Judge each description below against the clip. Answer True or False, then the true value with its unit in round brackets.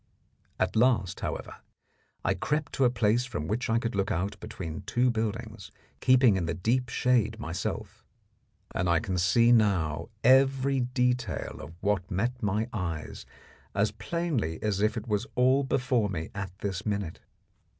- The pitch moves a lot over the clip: False (4.6 semitones)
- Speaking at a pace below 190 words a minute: True (160 wpm)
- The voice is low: True (110 Hz)